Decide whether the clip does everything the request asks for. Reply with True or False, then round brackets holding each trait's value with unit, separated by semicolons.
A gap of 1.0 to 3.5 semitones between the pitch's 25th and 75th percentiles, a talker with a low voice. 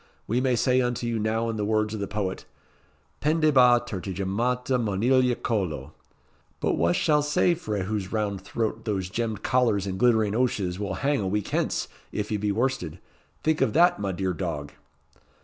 False (4.2 semitones; 110 Hz)